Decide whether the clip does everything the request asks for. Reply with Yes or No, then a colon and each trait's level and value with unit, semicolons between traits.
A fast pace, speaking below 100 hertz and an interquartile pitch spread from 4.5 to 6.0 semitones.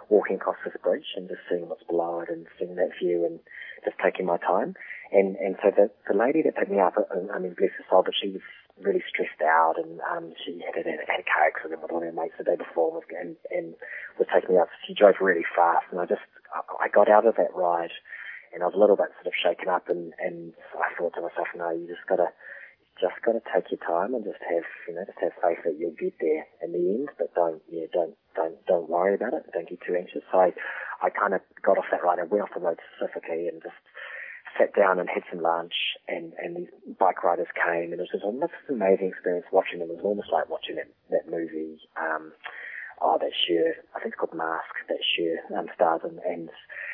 Yes: fast, 250 wpm; very low, 90 Hz; average, 5.2 semitones